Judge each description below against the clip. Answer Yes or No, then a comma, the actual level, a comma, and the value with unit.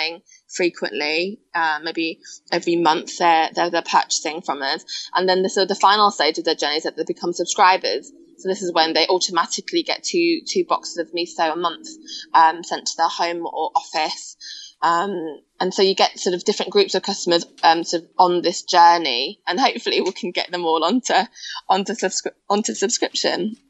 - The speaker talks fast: No, average, 190 wpm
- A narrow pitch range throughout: No, average, 3.4 semitones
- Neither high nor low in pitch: Yes, medium, 180 Hz